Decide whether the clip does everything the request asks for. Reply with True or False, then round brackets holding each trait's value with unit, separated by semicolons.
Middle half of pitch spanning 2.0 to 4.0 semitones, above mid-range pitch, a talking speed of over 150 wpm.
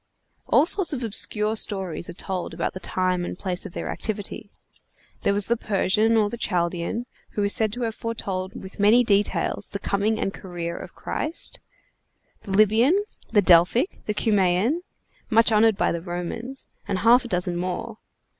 True (3.6 semitones; 205 Hz; 170 wpm)